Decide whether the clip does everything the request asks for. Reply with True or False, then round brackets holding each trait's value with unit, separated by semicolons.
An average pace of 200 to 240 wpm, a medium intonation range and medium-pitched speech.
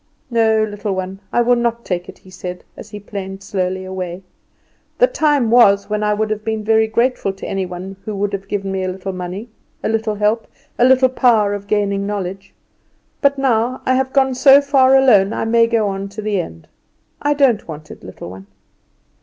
False (205 wpm; 3.6 semitones; 210 Hz)